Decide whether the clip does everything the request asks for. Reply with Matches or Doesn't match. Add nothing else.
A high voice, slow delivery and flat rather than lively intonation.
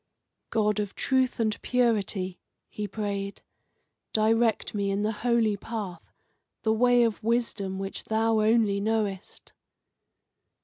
Matches